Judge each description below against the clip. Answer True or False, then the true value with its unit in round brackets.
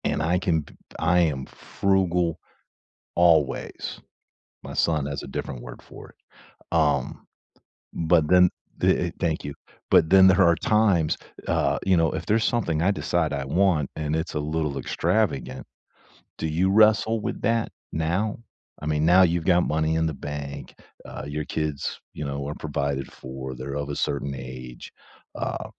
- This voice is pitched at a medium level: False (80 Hz)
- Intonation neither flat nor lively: True (4.1 semitones)